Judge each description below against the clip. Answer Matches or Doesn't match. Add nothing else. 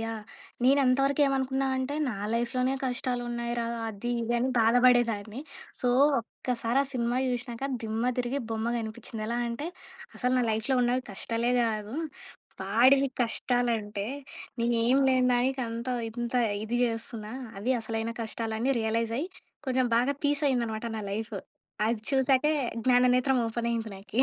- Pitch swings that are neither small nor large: Doesn't match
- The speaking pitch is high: Matches